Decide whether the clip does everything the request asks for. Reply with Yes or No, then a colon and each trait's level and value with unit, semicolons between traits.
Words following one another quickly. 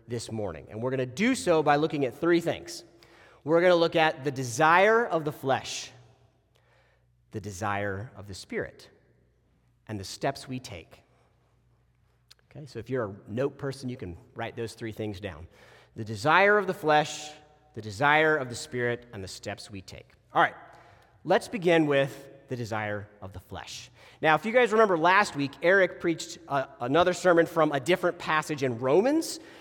No: average, 180 wpm